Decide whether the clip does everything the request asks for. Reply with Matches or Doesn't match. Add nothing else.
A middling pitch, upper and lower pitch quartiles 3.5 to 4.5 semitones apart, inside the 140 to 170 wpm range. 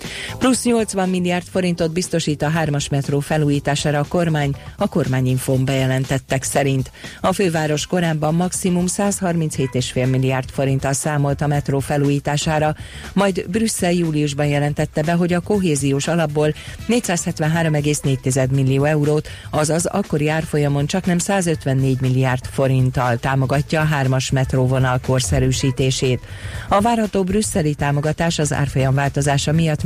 Doesn't match